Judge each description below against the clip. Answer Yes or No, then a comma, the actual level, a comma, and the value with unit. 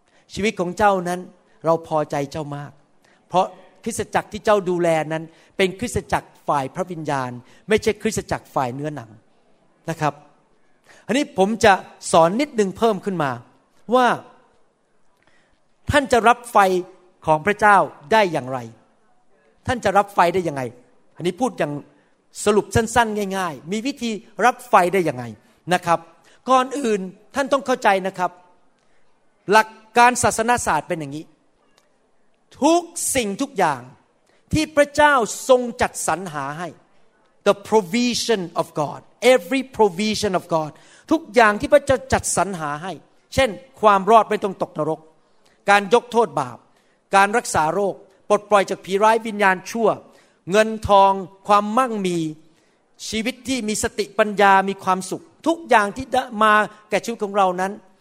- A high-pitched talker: Yes, high, 200 Hz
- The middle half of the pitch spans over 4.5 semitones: Yes, average, 5.1 semitones